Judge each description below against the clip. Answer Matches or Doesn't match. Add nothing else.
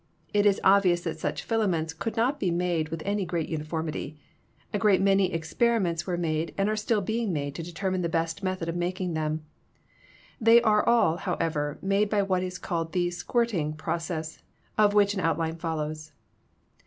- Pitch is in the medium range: Matches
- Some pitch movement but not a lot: Matches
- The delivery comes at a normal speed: Matches